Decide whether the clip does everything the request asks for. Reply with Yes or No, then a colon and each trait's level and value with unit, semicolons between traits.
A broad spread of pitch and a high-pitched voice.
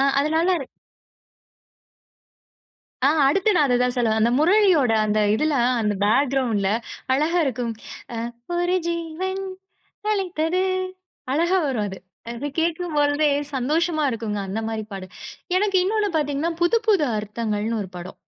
Yes: wide, 7.1 semitones; very high, 290 Hz